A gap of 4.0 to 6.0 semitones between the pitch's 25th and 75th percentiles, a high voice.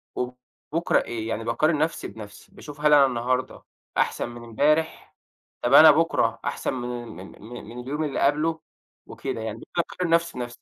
No: average, 4.5 semitones; low, 130 Hz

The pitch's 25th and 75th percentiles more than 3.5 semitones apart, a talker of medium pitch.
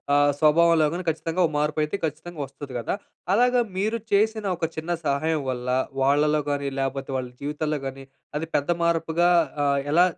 No: average, 3.0 semitones; medium, 155 Hz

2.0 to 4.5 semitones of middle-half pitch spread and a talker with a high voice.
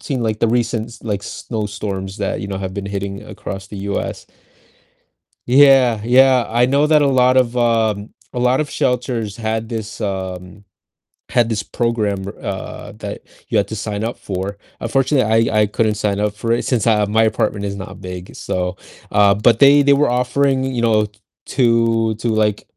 No: average, 3.3 semitones; low, 110 Hz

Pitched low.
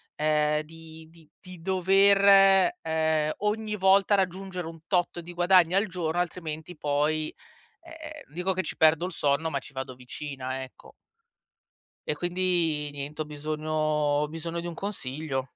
No: medium, 165 Hz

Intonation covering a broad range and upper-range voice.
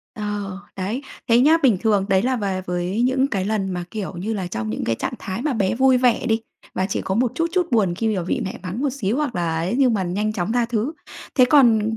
No: average, 4.7 semitones; high, 215 Hz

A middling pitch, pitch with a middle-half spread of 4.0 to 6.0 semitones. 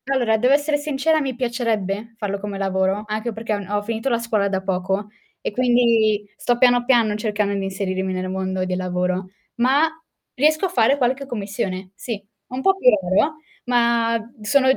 No: high, 220 Hz; average, 4.3 semitones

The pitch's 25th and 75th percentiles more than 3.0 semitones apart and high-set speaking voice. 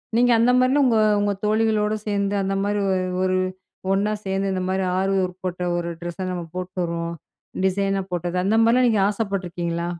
No: average, 2.7 semitones; high, 195 Hz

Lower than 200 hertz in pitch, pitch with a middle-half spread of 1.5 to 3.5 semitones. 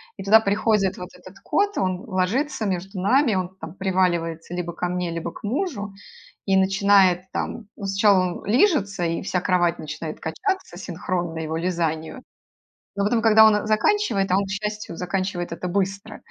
Yes: high, 190 Hz; average, 2.9 semitones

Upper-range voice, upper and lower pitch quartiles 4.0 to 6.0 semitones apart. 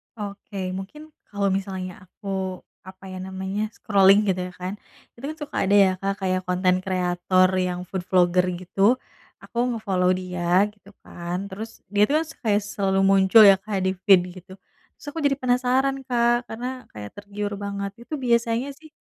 No: high, 195 Hz; average, 3.2 semitones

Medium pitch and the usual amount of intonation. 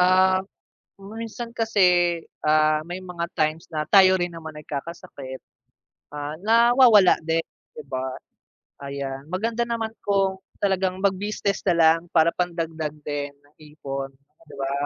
Yes: medium, 170 Hz; average, 4.2 semitones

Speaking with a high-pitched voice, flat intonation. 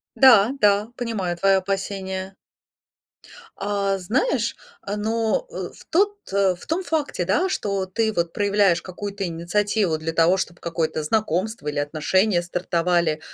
No: high, 195 Hz; average, 3.4 semitones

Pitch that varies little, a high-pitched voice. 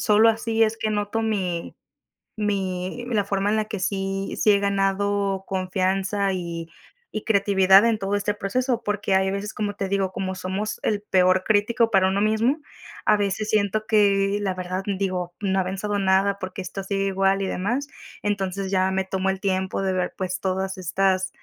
Yes: narrow, 1.6 semitones; high, 195 Hz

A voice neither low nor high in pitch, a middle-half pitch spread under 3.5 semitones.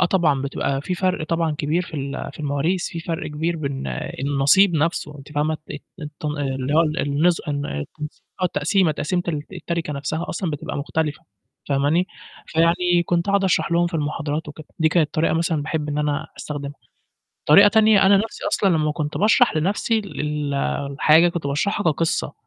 Yes: medium, 160 Hz; average, 3.0 semitones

